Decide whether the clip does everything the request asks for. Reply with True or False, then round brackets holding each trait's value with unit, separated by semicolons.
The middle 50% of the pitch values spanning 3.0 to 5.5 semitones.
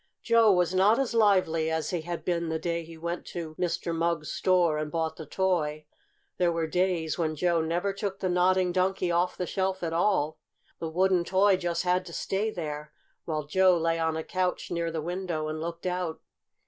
False (2.4 semitones)